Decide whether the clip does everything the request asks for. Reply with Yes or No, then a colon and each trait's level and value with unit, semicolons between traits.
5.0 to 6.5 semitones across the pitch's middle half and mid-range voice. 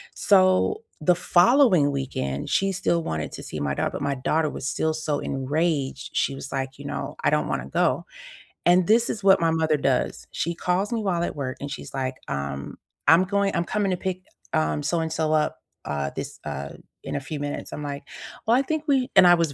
Yes: wide, 5.5 semitones; medium, 160 Hz